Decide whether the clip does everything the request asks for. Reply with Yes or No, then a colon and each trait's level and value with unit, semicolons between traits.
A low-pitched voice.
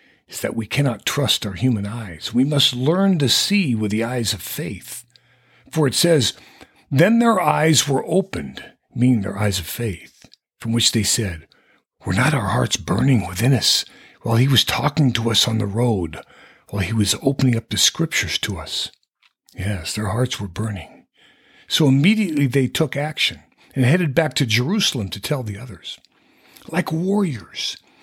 Yes: low, 125 Hz